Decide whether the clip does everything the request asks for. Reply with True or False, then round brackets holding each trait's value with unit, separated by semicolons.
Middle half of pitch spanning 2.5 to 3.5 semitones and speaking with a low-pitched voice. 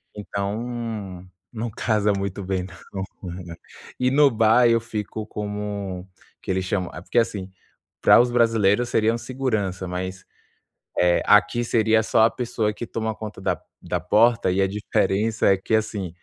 True (3.1 semitones; 105 Hz)